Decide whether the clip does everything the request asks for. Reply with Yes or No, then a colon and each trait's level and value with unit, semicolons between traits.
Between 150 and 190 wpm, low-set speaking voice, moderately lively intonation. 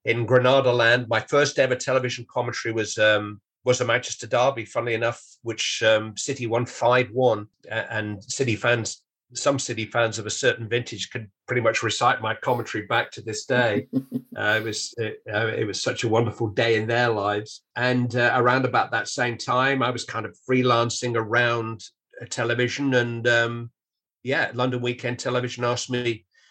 No: average, 175 wpm; low, 120 Hz; narrow, 1.6 semitones